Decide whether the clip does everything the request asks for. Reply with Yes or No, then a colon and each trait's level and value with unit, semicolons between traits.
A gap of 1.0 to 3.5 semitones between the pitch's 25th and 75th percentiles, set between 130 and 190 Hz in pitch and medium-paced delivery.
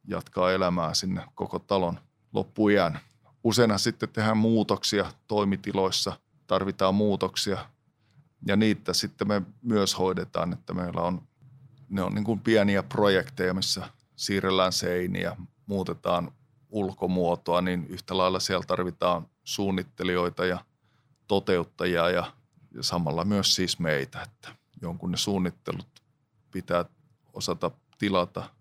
No: average, 3.1 semitones; low, 100 Hz; average, 115 wpm